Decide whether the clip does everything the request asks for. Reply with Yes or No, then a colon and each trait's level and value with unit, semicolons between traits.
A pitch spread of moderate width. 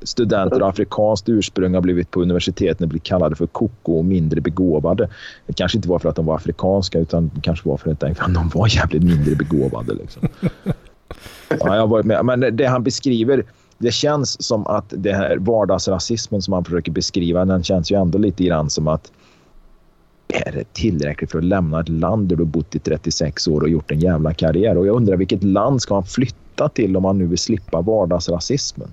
Yes: average, 3.5 semitones